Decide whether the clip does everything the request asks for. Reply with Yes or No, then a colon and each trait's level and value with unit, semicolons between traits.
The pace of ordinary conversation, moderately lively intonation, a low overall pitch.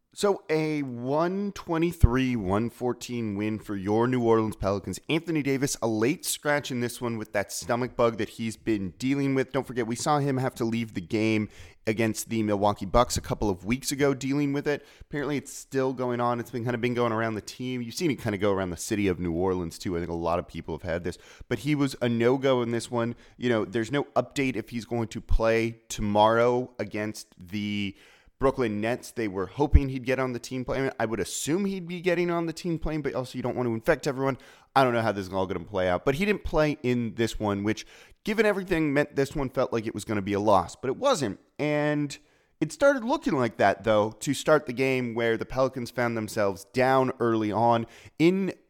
No: fast, 240 wpm; average, 4.3 semitones; low, 120 Hz